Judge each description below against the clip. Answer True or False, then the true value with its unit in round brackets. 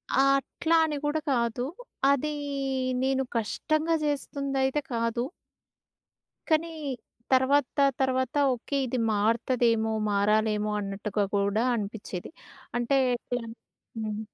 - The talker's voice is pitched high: True (240 Hz)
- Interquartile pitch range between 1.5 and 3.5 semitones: False (4.1 semitones)